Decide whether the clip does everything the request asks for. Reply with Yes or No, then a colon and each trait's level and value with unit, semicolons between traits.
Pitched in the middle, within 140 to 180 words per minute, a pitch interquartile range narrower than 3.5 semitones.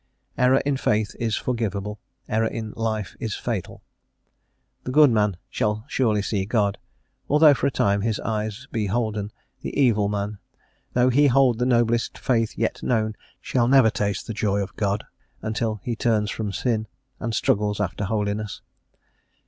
No: low, 110 Hz; average, 160 wpm; narrow, 2.6 semitones